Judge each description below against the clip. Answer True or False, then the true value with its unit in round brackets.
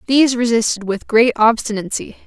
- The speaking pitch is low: False (230 Hz)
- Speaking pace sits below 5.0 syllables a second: False (5.5 syllables/s)